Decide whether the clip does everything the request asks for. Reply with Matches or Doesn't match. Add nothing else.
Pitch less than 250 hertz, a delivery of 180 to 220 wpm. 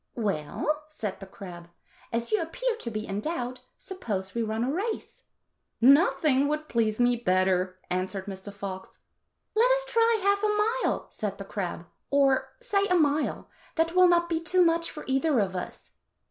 Doesn't match